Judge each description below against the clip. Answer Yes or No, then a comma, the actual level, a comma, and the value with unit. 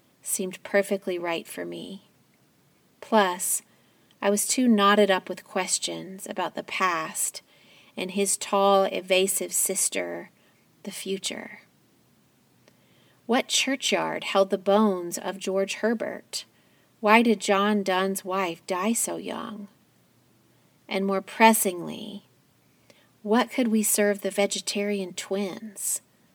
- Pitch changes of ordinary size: No, narrow, 1.8 semitones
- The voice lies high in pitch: Yes, high, 200 Hz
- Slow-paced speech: Yes, slow, 110 wpm